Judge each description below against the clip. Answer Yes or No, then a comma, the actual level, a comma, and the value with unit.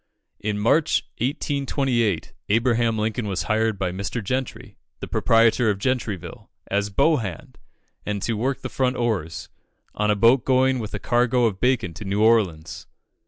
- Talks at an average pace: Yes, average, 160 wpm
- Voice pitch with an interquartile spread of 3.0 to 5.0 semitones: Yes, average, 3.6 semitones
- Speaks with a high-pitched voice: No, low, 115 Hz